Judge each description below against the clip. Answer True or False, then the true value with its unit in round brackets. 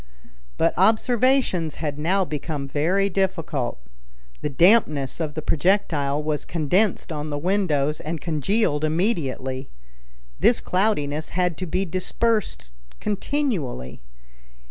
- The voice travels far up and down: False (4.9 semitones)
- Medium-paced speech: False (110 wpm)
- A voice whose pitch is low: False (165 Hz)